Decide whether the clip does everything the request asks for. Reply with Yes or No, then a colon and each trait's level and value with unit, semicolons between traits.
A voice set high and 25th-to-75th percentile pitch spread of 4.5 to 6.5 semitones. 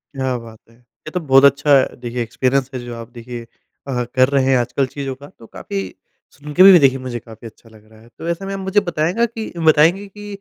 No: low, 135 Hz; average, 5.3 semitones